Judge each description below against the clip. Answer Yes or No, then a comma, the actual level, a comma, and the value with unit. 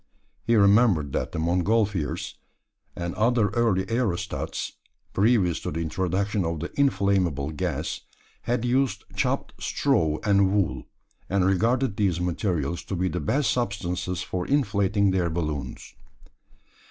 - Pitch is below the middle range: Yes, very low, 95 Hz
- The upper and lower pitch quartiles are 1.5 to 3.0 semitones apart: No, average, 4.3 semitones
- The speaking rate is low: Yes, slow, 130 wpm